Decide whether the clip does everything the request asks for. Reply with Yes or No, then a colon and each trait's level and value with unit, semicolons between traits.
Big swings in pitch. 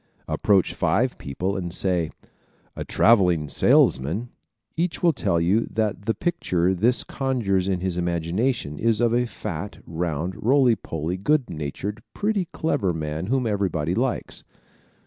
Yes: wide, 6.0 semitones